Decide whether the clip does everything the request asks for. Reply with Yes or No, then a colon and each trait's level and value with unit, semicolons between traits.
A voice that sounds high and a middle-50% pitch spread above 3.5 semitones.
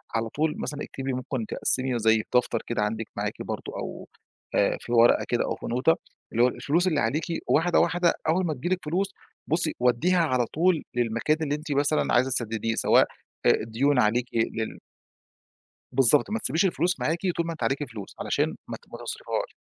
No: low, 135 Hz; wide, 5.4 semitones